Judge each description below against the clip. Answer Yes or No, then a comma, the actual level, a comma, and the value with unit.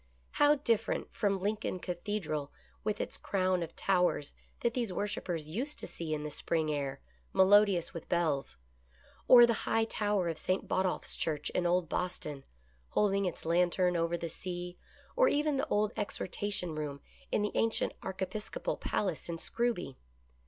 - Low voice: No, medium, 185 Hz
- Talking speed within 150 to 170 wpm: Yes, average, 160 wpm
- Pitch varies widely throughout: No, average, 3.9 semitones